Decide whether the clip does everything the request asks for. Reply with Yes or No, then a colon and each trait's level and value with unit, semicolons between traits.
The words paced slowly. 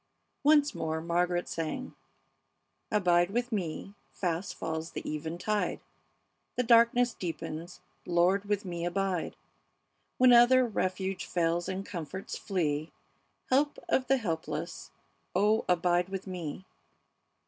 Yes: slow, 115 wpm